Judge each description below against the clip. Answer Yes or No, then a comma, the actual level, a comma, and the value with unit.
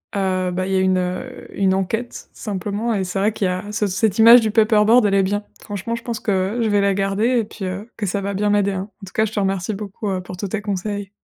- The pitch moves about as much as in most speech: No, narrow, 2.2 semitones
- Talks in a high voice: Yes, high, 200 Hz